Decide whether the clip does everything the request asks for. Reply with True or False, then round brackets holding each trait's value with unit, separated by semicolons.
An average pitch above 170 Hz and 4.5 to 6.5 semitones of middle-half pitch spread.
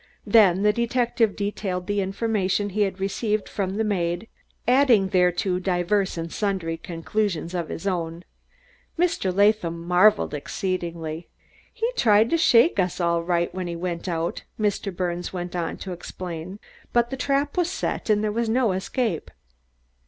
False (190 Hz; 3.6 semitones)